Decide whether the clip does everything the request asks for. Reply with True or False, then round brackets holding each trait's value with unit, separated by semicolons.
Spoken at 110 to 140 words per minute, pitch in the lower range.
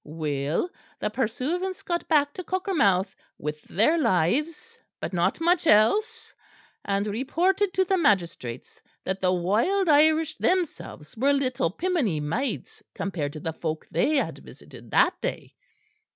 False (135 wpm; 255 Hz)